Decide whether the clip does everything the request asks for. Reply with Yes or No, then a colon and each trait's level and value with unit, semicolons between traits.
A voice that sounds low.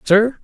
No: high, 215 Hz